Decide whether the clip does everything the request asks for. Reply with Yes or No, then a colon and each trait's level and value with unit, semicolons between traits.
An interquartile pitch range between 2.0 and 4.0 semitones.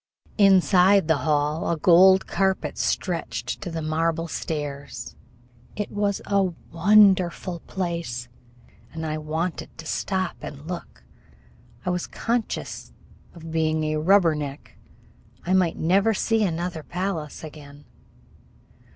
Yes: average, 3.5 semitones